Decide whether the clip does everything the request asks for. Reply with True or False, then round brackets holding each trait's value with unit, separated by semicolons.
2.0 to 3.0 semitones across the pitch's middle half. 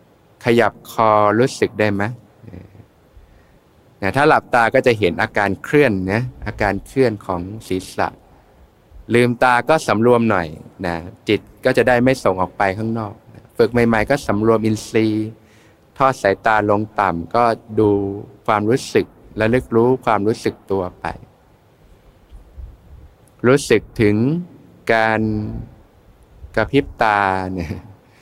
True (2.7 semitones)